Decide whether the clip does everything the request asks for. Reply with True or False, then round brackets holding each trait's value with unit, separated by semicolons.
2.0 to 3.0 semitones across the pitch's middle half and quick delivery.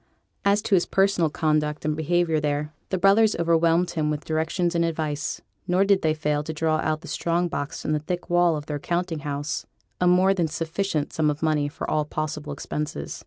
True (2.6 semitones; 210 wpm)